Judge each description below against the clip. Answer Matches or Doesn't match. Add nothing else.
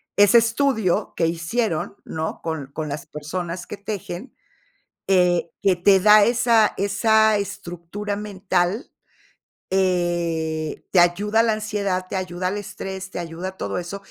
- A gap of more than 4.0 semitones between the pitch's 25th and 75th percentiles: Doesn't match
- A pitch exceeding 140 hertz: Matches